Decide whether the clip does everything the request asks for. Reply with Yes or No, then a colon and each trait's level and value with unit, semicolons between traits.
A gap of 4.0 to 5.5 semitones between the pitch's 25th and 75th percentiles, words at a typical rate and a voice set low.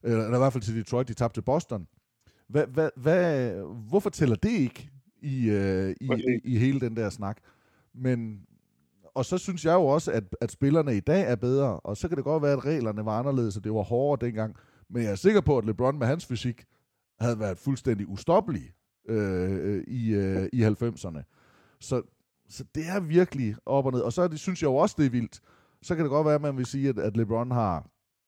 No: average, 4.5 semitones; fast, 220 wpm; low, 120 Hz